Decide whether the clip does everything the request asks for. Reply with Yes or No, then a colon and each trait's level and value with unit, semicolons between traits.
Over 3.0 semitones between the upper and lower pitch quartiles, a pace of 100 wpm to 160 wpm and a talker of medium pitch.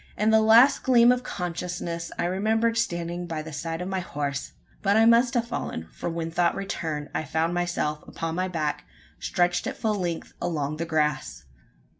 No: average, 5.1 semitones; average, 185 wpm; medium, 175 Hz